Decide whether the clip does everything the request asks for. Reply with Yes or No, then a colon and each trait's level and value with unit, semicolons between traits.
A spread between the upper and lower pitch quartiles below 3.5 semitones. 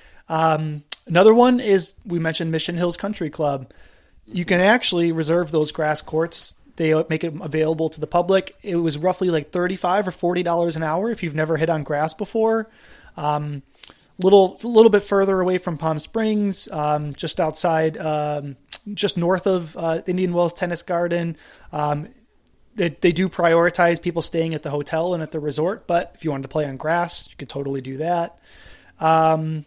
Yes: average, 2.8 semitones